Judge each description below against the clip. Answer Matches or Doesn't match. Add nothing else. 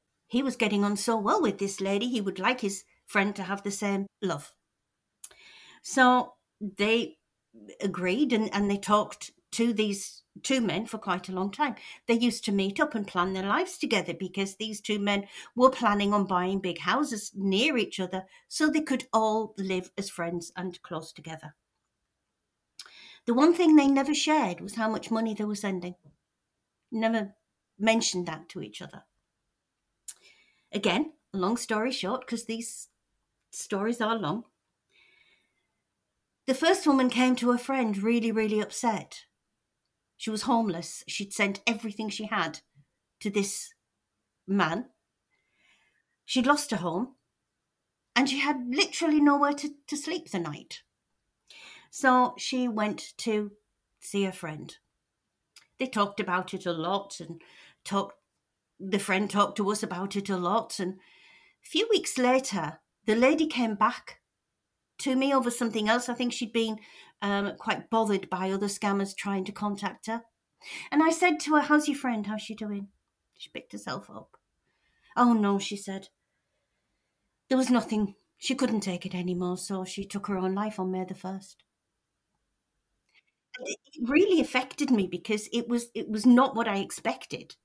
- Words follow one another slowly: Doesn't match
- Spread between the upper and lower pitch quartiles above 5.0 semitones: Doesn't match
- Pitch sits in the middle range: Doesn't match